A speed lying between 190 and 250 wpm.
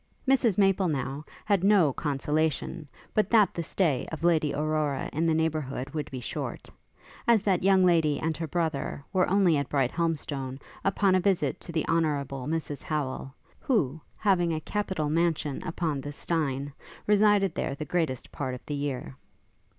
No: average, 165 wpm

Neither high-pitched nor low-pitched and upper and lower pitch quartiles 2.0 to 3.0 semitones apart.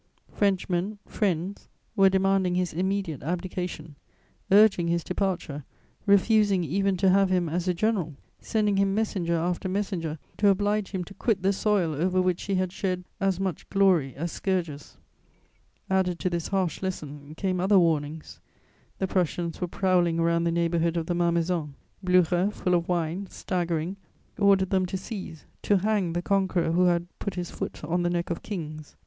Yes: medium, 180 Hz; narrow, 2.4 semitones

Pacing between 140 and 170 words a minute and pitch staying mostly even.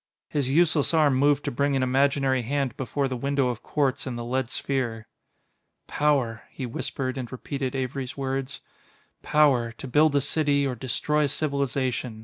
Yes: average, 165 wpm; narrow, 2.0 semitones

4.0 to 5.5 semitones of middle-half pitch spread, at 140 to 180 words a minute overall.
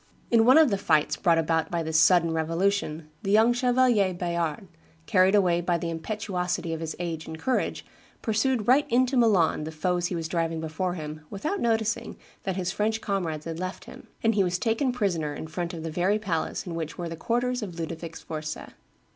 No: average, 4.9 semitones; average, 200 wpm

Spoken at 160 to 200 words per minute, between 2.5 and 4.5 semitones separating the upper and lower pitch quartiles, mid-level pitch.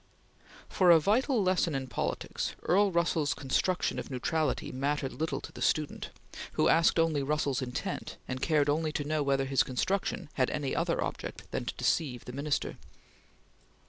Yes: average, 165 wpm; average, 3.8 semitones; medium, 150 Hz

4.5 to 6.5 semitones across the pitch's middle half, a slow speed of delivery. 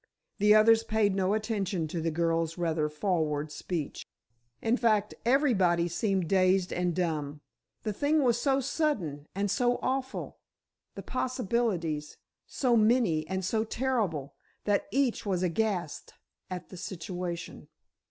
Yes: average, 5.3 semitones; slow, 125 wpm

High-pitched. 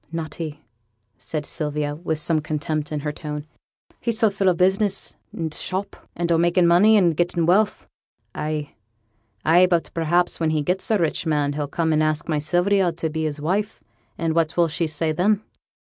No: medium, 165 Hz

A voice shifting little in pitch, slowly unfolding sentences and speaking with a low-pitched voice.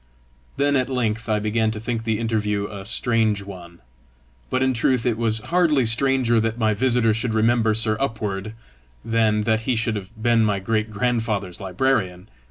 No: narrow, 2.0 semitones; average, 175 wpm; low, 110 Hz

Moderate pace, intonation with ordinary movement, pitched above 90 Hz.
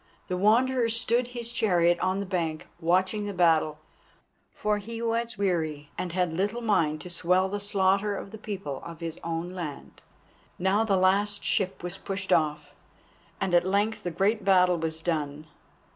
Yes: average, 170 wpm; average, 3.5 semitones; high, 190 Hz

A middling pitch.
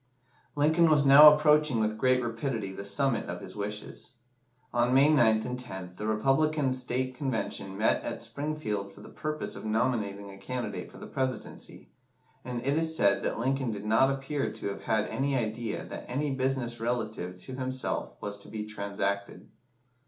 No: low, 120 Hz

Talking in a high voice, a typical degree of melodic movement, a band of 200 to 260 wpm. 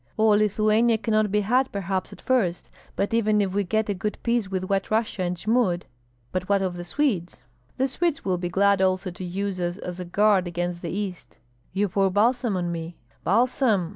Yes: high, 195 Hz; average, 3.1 semitones; fast, 205 wpm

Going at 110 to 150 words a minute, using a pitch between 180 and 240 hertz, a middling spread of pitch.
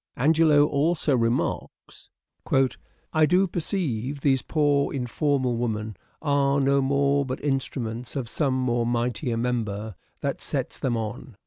No: slow, 135 wpm; low, 135 Hz; average, 3.2 semitones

